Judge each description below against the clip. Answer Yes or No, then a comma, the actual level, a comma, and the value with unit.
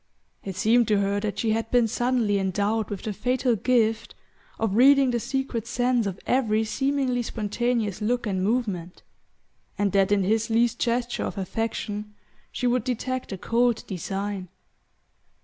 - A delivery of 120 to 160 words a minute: Yes, average, 155 wpm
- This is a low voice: No, high, 225 Hz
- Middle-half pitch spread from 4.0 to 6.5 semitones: No, average, 3.2 semitones